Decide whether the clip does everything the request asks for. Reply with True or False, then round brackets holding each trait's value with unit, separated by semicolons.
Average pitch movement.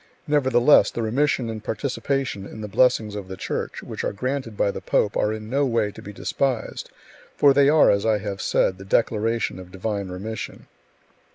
True (4.4 semitones)